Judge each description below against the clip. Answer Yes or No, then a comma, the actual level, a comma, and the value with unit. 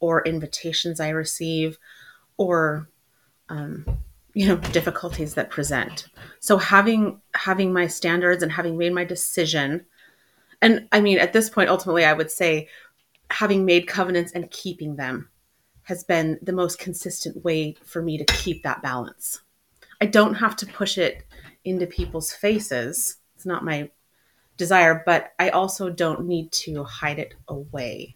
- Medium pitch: Yes, medium, 170 Hz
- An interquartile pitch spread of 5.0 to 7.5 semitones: No, average, 3.0 semitones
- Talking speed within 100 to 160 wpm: Yes, average, 150 wpm